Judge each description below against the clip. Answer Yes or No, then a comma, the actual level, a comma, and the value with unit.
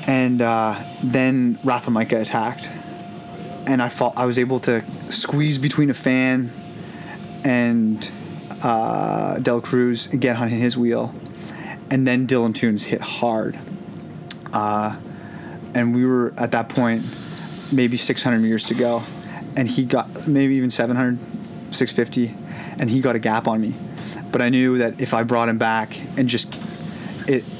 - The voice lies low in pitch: Yes, low, 125 Hz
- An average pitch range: Yes, average, 3.1 semitones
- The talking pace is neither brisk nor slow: Yes, average, 150 wpm